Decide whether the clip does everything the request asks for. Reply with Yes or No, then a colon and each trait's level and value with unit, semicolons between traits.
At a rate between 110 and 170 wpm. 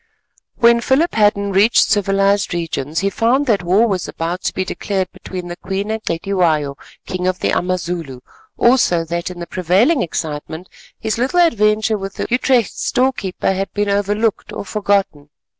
Yes: average, 165 wpm